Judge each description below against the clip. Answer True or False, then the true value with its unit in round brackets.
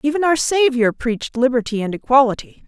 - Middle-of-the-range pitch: False (260 Hz)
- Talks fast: False (155 wpm)